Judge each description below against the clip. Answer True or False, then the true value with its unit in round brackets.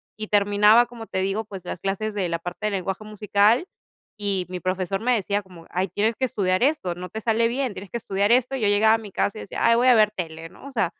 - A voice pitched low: False (205 Hz)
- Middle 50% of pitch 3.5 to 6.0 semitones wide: False (3.0 semitones)